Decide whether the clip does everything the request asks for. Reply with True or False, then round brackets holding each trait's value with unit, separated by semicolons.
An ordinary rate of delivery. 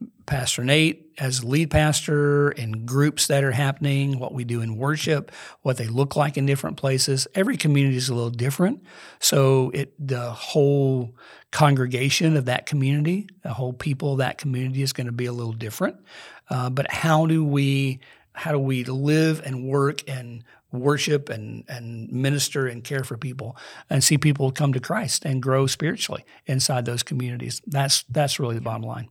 True (180 wpm)